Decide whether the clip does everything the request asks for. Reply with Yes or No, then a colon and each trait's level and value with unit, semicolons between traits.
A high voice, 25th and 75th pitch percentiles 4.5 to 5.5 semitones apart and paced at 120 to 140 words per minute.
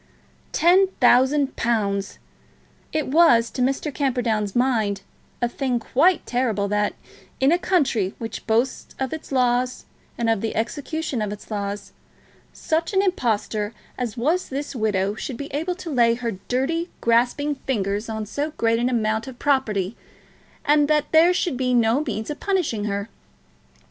No: high, 245 Hz; average, 4.9 semitones; average, 155 wpm